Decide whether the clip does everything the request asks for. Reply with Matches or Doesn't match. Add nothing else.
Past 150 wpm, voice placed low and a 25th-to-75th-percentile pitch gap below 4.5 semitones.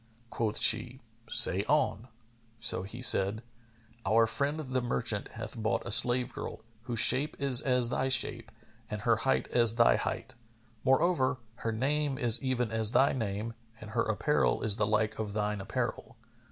Matches